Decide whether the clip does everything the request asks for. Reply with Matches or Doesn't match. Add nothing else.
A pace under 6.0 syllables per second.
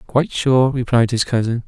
Matches